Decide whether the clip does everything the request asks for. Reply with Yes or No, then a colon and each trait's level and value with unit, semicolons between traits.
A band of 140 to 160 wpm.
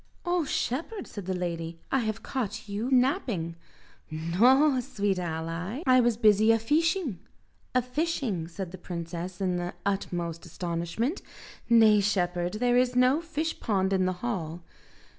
Yes: average, 145 wpm